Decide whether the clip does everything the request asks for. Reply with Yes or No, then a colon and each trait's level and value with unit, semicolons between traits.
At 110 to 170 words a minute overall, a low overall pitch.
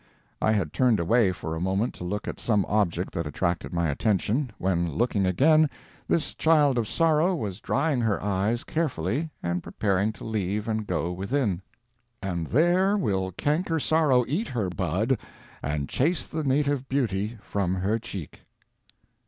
Yes: average, 160 wpm; low, 110 Hz